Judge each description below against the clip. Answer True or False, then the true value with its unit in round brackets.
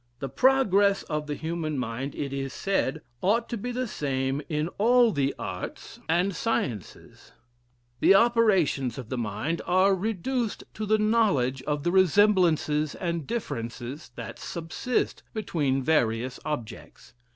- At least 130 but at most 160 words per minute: True (140 wpm)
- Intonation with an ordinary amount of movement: False (7.3 semitones)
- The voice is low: False (165 Hz)